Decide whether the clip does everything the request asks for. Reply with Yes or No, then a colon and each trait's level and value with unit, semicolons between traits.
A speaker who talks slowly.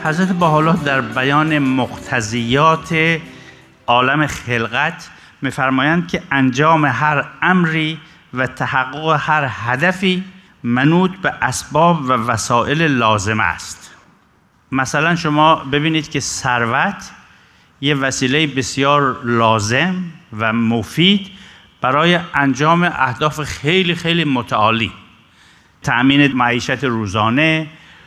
Yes: slow, 90 wpm